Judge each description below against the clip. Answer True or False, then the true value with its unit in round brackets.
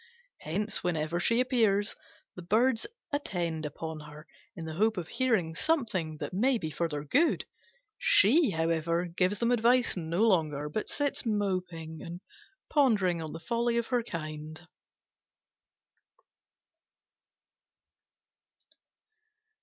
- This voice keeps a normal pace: False (120 wpm)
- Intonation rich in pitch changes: True (6.3 semitones)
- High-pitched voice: False (180 Hz)